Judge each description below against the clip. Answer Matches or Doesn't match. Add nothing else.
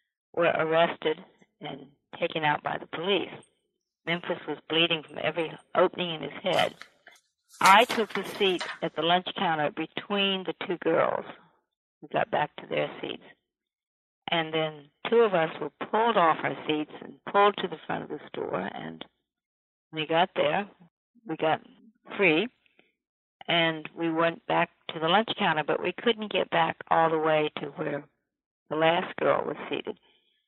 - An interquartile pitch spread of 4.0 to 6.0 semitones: Doesn't match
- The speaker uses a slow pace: Doesn't match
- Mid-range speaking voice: Matches